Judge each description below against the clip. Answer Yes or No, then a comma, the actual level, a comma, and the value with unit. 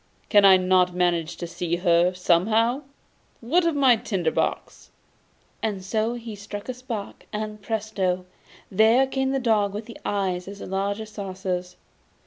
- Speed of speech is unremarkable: Yes, average, 150 wpm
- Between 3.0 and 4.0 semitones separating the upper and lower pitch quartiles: Yes, average, 3.6 semitones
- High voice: Yes, high, 205 Hz